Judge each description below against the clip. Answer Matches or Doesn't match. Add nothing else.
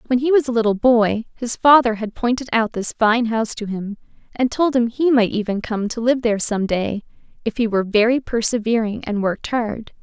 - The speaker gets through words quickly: Matches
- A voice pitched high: Matches